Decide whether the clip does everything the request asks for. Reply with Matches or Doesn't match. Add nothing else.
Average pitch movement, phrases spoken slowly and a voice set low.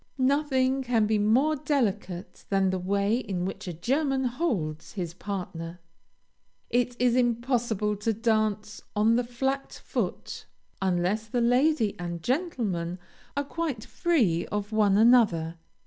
Doesn't match